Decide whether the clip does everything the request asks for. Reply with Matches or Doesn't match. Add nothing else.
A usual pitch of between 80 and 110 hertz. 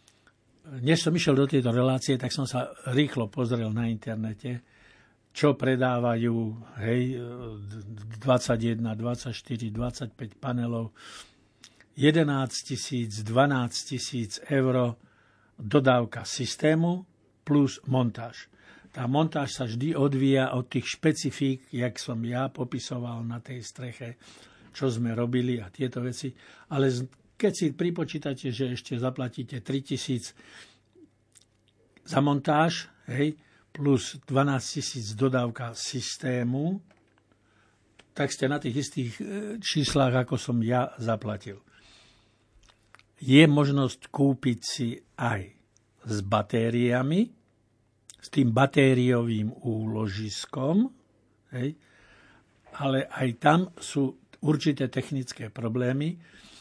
Doesn't match